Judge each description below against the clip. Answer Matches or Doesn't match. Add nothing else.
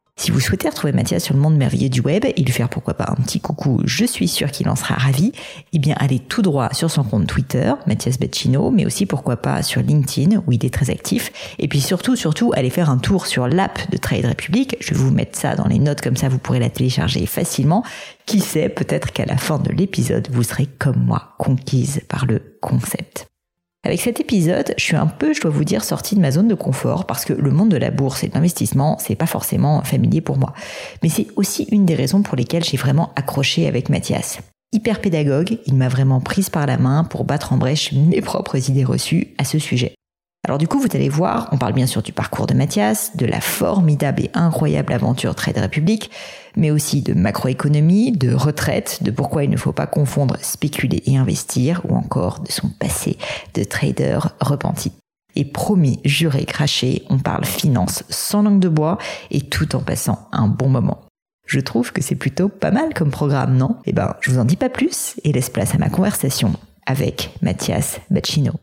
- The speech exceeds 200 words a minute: Matches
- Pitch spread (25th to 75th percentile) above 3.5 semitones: Matches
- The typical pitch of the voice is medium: Matches